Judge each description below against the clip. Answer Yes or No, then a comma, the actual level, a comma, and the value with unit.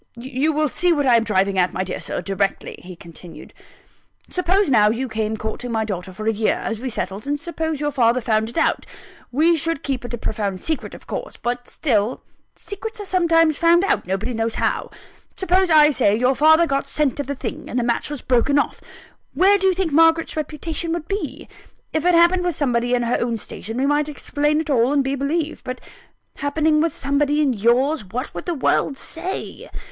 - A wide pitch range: Yes, wide, 5.7 semitones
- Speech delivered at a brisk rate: Yes, fast, 210 wpm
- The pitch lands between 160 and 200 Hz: No, very high, 275 Hz